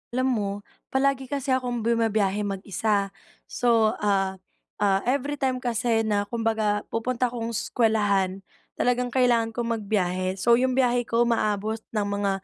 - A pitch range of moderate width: Yes, average, 3.3 semitones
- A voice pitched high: Yes, high, 225 Hz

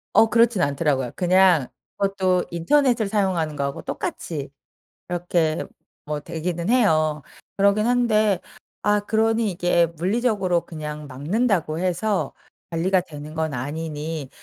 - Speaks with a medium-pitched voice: Yes, medium, 175 Hz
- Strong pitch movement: No, average, 5.0 semitones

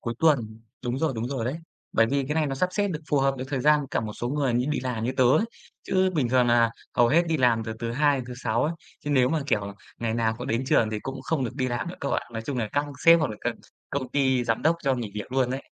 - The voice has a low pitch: Yes, low, 130 Hz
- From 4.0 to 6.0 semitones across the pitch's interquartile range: No, average, 3.6 semitones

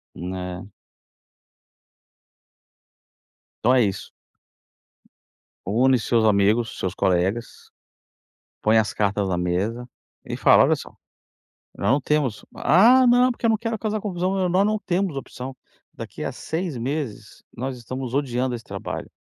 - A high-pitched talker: No, low, 125 Hz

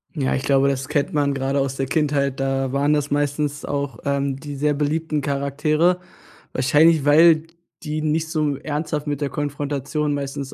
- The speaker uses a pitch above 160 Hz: No, medium, 145 Hz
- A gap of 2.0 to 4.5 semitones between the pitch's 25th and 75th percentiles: No, narrow, 1.6 semitones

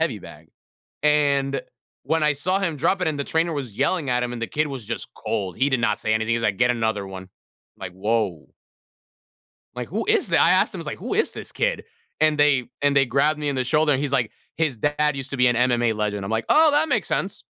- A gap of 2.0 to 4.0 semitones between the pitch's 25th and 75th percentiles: No, average, 4.7 semitones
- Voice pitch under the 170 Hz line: Yes, low, 135 Hz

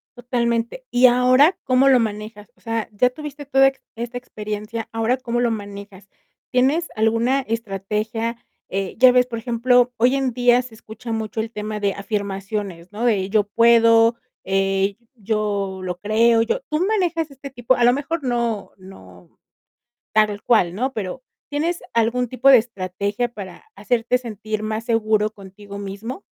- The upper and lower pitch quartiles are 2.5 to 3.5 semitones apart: Yes, average, 3.2 semitones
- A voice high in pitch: Yes, high, 230 Hz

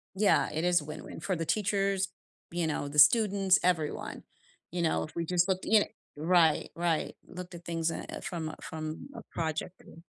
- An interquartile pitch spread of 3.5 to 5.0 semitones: No, average, 2.8 semitones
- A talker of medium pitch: Yes, medium, 170 Hz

